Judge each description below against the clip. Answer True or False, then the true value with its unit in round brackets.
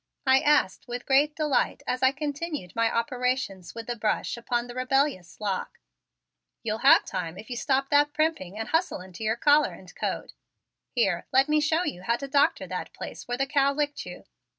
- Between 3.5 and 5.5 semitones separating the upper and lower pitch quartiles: True (4.5 semitones)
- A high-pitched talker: True (255 Hz)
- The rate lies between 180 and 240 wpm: True (195 wpm)